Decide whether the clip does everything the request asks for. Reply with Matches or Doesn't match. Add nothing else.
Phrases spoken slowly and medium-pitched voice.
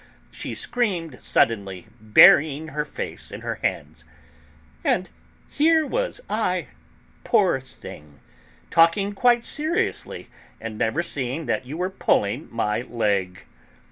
Matches